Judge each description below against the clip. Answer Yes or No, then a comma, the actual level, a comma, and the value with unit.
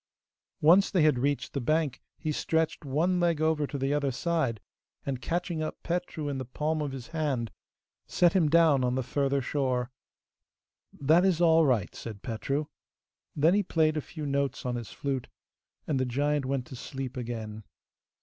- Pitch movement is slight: No, average, 3.7 semitones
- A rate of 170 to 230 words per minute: Yes, average, 180 wpm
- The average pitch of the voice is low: No, medium, 145 Hz